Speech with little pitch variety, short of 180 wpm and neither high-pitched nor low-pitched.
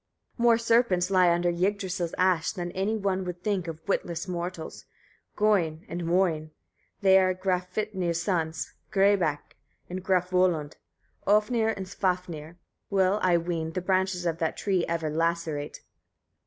Yes: narrow, 2.3 semitones; average, 140 wpm; medium, 180 Hz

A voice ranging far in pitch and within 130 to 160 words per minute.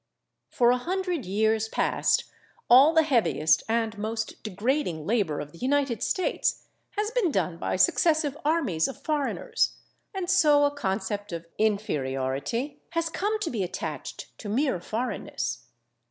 Yes: wide, 8.1 semitones; average, 140 wpm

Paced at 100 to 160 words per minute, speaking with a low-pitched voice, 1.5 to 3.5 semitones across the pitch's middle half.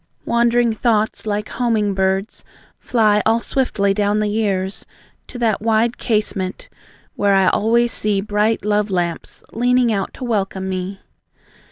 No: average, 140 wpm; high, 210 Hz; average, 2.8 semitones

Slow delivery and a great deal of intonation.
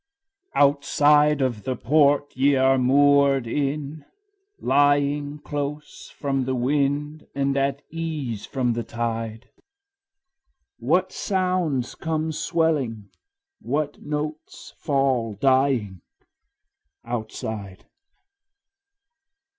No: slow, 90 wpm; average, 2.8 semitones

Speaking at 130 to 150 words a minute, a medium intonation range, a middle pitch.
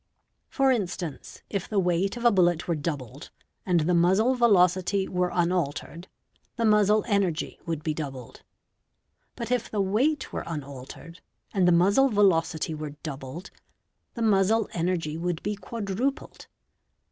Yes: average, 140 wpm; average, 4.3 semitones; medium, 180 Hz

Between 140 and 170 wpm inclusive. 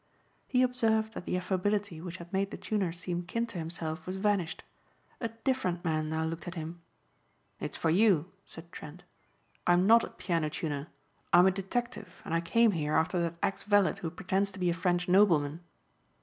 No: average, 190 wpm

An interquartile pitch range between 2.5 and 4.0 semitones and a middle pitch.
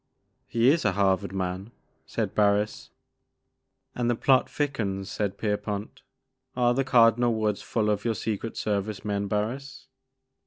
No: average, 3.0 semitones; low, 105 Hz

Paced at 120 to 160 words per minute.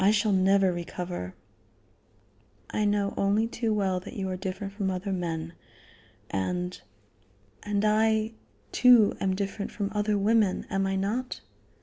Yes: average, 140 wpm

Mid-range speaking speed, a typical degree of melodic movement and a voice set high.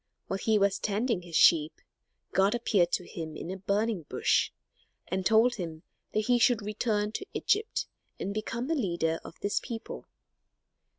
Yes: average, 165 wpm; average, 4.1 semitones; high, 205 Hz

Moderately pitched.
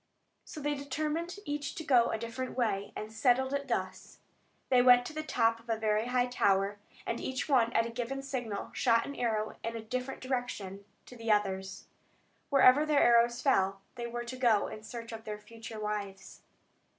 No: high, 235 Hz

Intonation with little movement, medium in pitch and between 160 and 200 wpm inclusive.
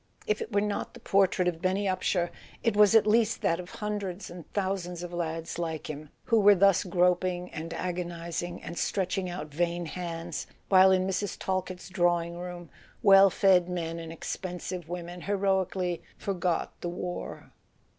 Yes: narrow, 2.0 semitones; medium, 180 Hz; average, 165 wpm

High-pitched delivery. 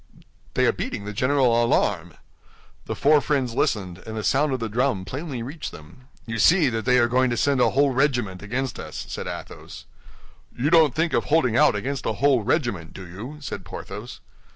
No: low, 125 Hz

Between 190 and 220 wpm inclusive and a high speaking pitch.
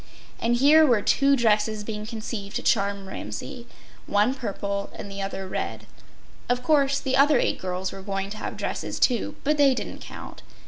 No: average, 175 wpm; high, 220 Hz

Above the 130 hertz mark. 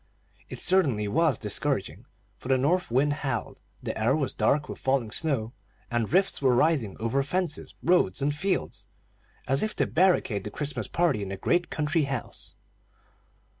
Yes: medium, 140 Hz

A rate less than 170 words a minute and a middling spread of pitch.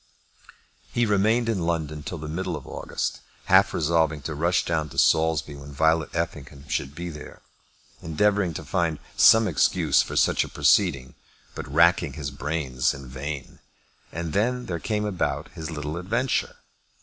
Yes: average, 160 wpm; average, 3.6 semitones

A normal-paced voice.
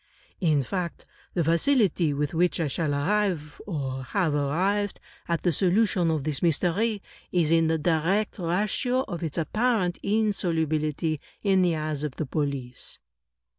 Yes: average, 150 wpm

